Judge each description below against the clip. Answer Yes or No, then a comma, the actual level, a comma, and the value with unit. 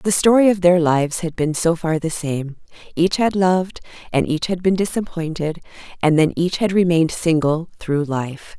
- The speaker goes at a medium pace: Yes, average, 190 wpm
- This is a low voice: No, medium, 170 Hz